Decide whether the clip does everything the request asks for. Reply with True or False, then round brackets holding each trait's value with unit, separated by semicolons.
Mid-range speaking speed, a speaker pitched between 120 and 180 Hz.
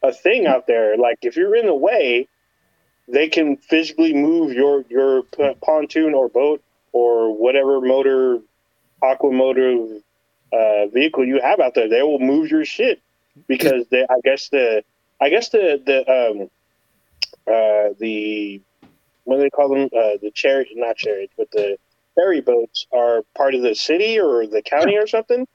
True (165 wpm; 140 Hz)